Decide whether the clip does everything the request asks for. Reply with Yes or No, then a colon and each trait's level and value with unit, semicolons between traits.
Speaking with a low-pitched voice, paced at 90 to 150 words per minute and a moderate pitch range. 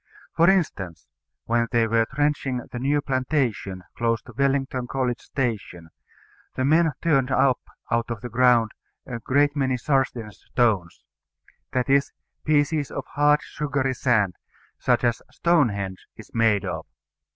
Yes: low, 125 Hz; average, 140 wpm; average, 3.6 semitones